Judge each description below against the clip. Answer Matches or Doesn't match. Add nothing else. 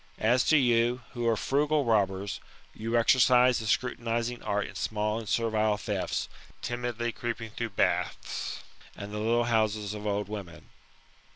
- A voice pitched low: Matches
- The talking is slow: Doesn't match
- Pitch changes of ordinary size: Doesn't match